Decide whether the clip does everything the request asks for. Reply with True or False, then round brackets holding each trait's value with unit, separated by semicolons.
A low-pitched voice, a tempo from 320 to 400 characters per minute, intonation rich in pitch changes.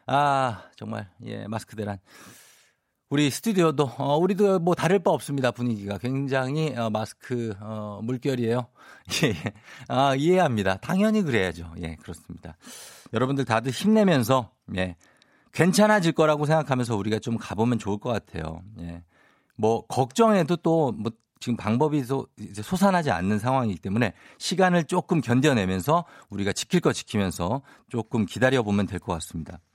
True (120 Hz; 325 characters per minute; 6.3 semitones)